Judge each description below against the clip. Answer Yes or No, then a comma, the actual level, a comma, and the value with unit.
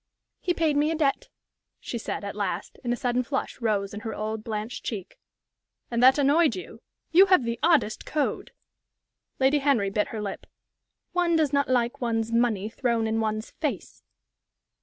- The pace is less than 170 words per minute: No, average, 175 wpm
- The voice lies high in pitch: Yes, high, 235 Hz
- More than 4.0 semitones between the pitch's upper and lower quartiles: Yes, average, 4.8 semitones